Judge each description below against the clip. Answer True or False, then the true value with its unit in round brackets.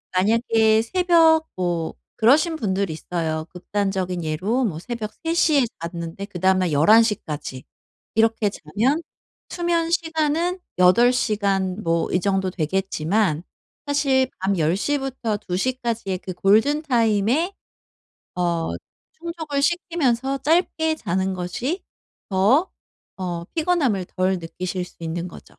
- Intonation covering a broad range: True (7.8 semitones)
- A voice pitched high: True (210 Hz)